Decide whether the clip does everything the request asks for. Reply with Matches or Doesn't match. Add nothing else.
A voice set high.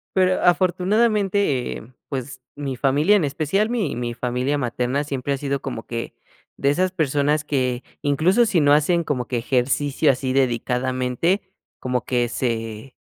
Doesn't match